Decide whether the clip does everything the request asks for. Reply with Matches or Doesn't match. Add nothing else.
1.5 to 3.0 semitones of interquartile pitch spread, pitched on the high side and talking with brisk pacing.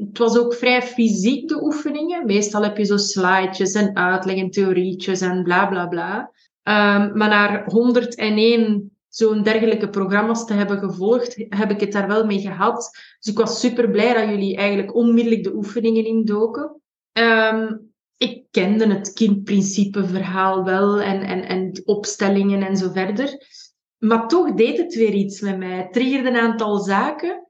Doesn't match